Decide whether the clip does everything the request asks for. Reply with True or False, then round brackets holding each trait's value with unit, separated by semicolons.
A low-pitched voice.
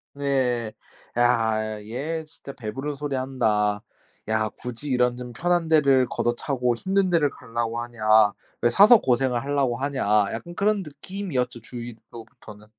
True (125 Hz)